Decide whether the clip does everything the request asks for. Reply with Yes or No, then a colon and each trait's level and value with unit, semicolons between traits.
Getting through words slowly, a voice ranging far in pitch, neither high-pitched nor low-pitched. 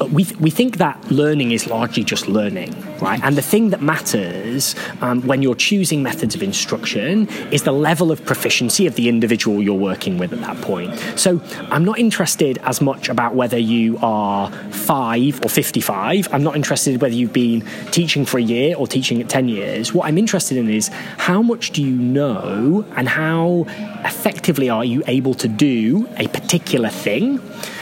No: average, 190 wpm; wide, 7.2 semitones; medium, 145 Hz